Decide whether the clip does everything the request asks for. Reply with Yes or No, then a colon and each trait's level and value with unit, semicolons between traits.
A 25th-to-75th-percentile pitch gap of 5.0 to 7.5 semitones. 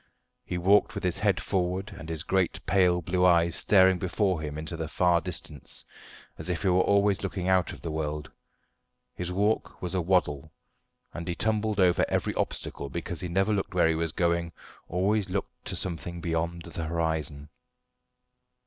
No: narrow, 2.4 semitones